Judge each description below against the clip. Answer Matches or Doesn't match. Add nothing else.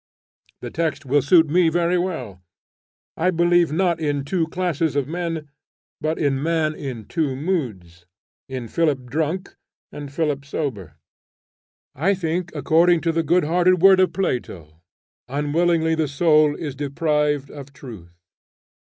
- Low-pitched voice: Doesn't match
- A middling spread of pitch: Matches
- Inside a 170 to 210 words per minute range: Doesn't match